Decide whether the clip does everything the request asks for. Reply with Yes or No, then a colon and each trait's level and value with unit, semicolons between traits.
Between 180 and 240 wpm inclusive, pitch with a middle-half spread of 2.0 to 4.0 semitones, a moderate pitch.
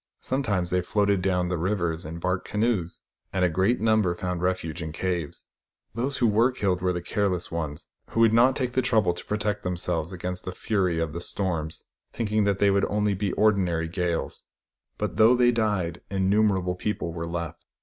No: average, 190 wpm; average, 3.3 semitones; very low, 95 Hz